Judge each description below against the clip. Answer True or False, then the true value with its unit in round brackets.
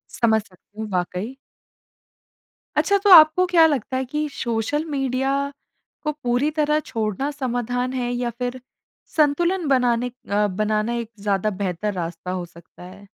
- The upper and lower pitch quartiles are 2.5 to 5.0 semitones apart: False (5.6 semitones)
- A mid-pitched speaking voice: False (245 Hz)